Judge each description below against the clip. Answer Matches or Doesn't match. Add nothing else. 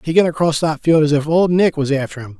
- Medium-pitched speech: Matches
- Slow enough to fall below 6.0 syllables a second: Doesn't match